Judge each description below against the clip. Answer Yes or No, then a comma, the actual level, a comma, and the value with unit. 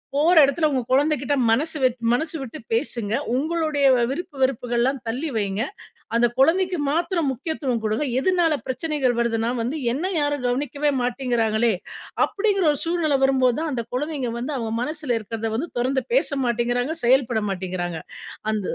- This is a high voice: Yes, very high, 265 Hz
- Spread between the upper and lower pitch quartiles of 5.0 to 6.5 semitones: No, average, 4.6 semitones